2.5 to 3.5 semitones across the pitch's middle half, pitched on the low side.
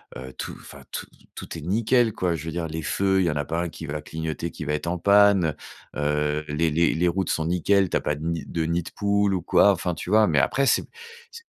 No: average, 3.9 semitones; very low, 85 Hz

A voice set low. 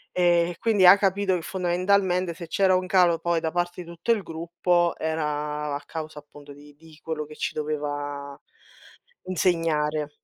No: medium, 165 Hz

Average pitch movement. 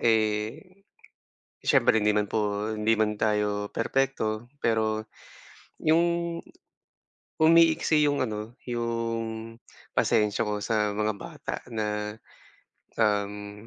No: narrow, 1.9 semitones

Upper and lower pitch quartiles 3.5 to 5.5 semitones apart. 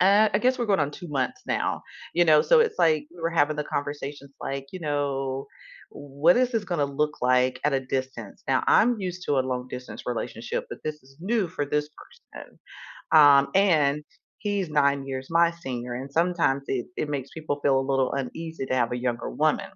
Yes: average, 4.2 semitones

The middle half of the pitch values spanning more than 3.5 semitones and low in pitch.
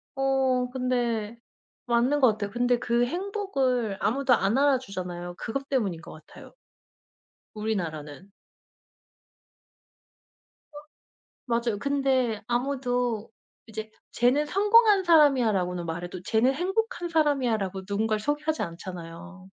No: average, 5.3 semitones; high, 240 Hz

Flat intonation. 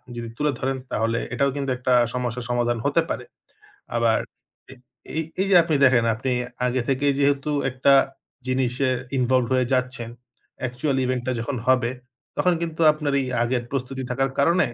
Yes: narrow, 2.3 semitones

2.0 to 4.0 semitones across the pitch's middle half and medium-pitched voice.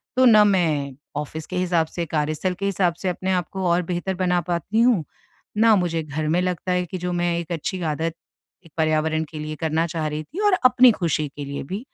Yes: average, 3.0 semitones; medium, 175 Hz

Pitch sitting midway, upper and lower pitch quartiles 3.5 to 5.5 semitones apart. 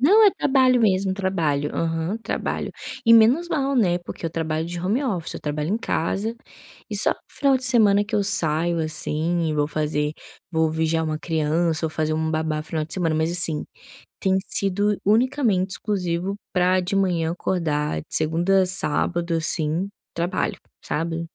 Yes: medium, 175 Hz; average, 4.0 semitones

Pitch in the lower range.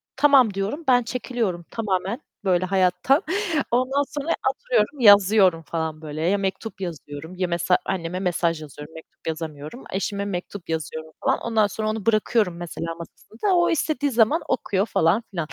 No: high, 195 Hz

